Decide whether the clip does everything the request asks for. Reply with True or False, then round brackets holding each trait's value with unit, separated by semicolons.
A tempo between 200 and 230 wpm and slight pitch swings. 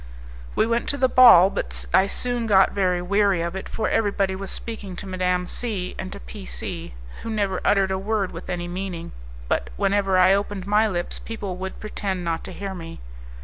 True (205 wpm; 2.3 semitones)